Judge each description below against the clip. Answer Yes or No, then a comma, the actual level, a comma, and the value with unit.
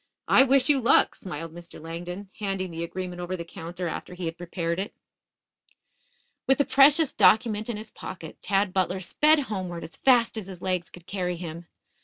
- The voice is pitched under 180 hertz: No, medium, 185 Hz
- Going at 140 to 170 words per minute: No, average, 185 wpm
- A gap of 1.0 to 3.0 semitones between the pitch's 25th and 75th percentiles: No, average, 4.2 semitones